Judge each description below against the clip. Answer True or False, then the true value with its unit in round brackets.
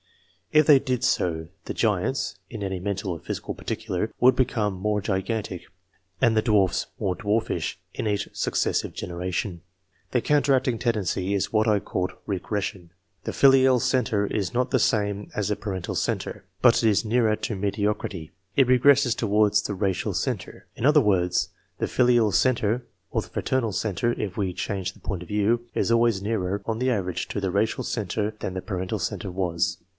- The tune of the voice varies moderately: True (3.6 semitones)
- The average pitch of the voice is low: True (105 Hz)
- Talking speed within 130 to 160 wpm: False (180 wpm)